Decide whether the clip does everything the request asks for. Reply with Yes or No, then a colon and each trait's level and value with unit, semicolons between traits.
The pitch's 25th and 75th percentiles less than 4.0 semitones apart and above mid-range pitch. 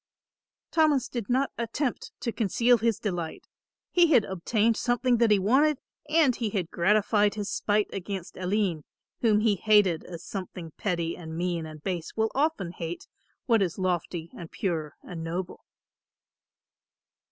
No: average, 5.0 semitones; high, 205 Hz